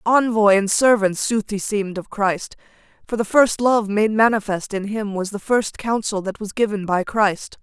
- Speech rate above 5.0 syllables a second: No, 4.6 syllables/s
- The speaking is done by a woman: Yes, female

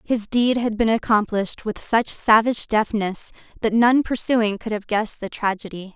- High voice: Yes, high, 220 Hz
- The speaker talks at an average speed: Yes, average, 170 wpm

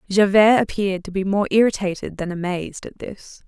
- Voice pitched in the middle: No, high, 195 Hz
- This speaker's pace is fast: No, average, 170 wpm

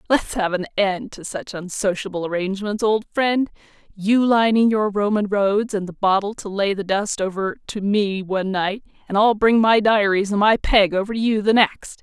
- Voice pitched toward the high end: Yes, high, 205 Hz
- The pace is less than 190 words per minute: No, average, 200 wpm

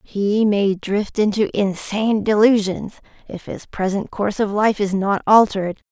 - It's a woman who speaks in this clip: Yes, female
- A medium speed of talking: Yes, average, 150 wpm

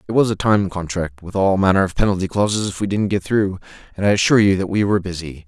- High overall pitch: No, very low, 95 Hz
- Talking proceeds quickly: Yes, fast, 265 wpm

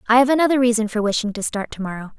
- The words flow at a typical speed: No, fast, 275 wpm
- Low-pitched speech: No, high, 230 Hz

